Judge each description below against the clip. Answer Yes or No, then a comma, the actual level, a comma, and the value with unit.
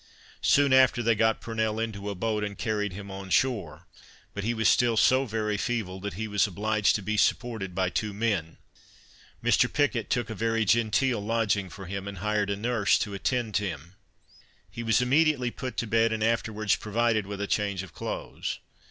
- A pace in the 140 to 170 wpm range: No, average, 190 wpm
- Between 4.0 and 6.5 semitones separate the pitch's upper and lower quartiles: No, narrow, 2.5 semitones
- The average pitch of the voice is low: Yes, low, 110 Hz